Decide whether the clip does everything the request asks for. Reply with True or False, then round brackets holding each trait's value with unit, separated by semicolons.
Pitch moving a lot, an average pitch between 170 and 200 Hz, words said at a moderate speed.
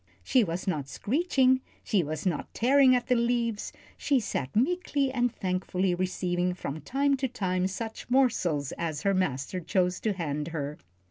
True (6.6 semitones; 190 Hz; 160 wpm)